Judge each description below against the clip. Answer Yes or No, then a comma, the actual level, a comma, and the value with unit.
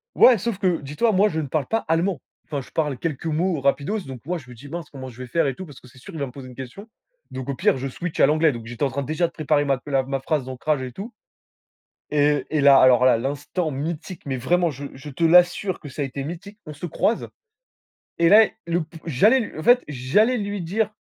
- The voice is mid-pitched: Yes, medium, 150 Hz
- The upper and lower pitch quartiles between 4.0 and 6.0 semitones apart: Yes, average, 4.7 semitones